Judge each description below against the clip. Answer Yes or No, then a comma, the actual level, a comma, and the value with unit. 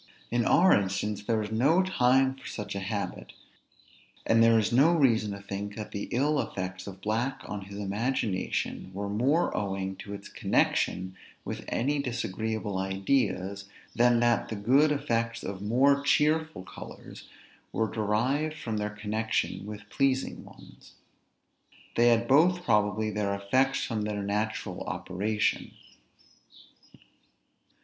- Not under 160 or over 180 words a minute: No, average, 140 wpm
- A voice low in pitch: Yes, low, 110 Hz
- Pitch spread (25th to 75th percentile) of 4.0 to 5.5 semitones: Yes, average, 4.5 semitones